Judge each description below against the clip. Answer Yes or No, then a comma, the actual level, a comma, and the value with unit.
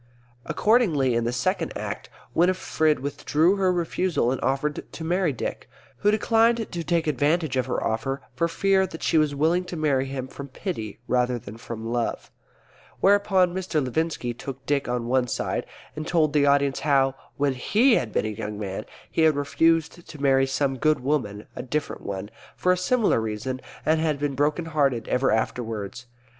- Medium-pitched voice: Yes, medium, 145 Hz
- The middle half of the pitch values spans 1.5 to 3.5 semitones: No, average, 4.9 semitones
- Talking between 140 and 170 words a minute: No, average, 180 wpm